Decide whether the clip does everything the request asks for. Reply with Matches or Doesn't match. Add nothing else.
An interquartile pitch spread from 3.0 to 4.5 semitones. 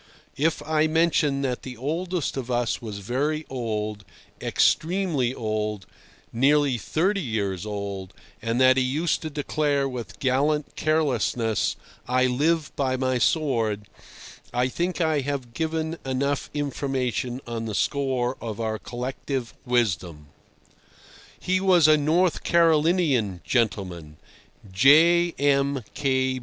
Doesn't match